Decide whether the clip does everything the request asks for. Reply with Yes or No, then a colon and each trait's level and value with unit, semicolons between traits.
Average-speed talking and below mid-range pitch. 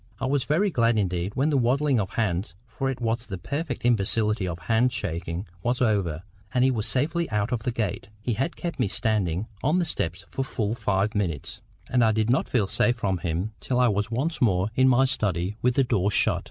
No: fast, 215 wpm; low, 115 Hz